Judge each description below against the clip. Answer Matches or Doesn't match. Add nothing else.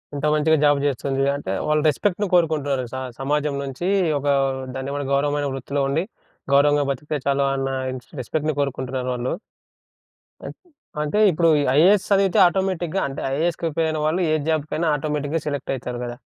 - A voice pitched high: Doesn't match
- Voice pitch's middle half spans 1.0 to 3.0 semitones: Matches